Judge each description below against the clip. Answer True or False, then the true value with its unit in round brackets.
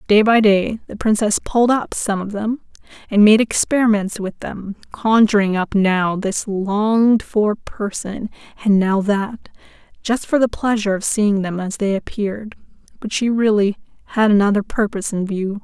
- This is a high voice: True (210 Hz)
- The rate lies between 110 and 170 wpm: True (165 wpm)